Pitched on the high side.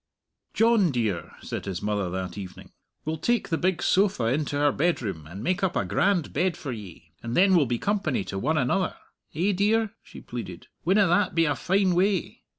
No: medium, 160 Hz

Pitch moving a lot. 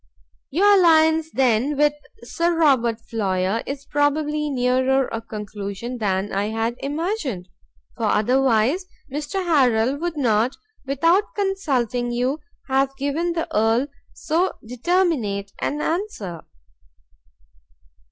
Yes: wide, 5.9 semitones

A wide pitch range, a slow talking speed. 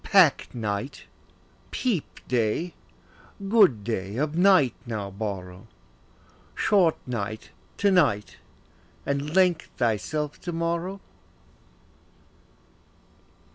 Yes: wide, 8.3 semitones; slow, 85 wpm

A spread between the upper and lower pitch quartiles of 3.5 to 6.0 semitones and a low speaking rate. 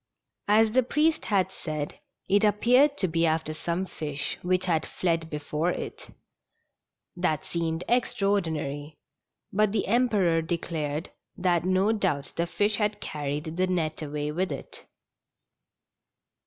Yes: average, 4.6 semitones; slow, 130 wpm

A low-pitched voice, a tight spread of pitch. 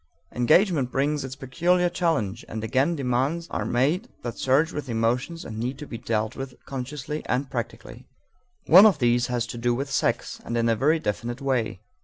No: low, 130 Hz; average, 4.1 semitones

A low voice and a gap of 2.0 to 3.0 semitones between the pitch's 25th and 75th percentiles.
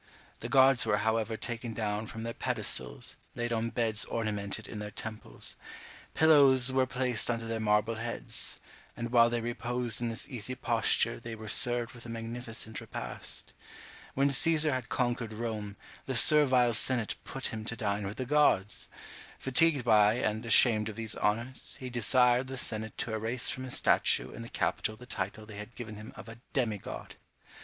Yes: low, 115 Hz; narrow, 2.4 semitones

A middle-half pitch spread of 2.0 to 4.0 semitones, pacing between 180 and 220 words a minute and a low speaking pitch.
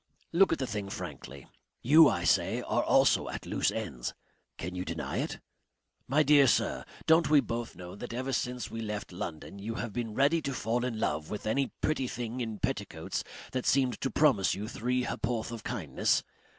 No: average, 4.5 semitones; average, 190 wpm; low, 120 Hz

